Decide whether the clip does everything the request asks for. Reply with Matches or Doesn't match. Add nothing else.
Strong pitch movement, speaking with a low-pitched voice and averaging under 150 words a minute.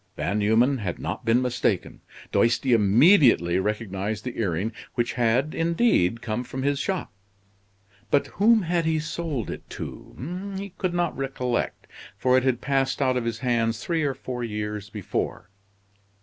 Doesn't match